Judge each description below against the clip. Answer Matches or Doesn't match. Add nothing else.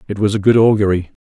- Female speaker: Doesn't match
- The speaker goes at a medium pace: Doesn't match